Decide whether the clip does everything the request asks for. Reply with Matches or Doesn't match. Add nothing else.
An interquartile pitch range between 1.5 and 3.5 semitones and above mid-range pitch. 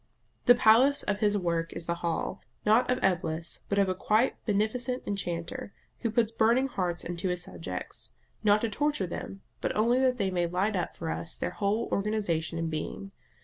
Doesn't match